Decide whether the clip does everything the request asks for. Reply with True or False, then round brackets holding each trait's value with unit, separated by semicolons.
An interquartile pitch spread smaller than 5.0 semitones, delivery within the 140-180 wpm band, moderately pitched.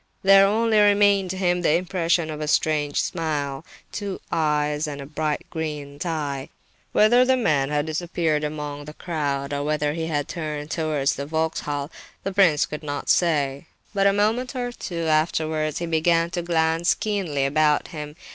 True (3.2 semitones; 170 wpm; 160 Hz)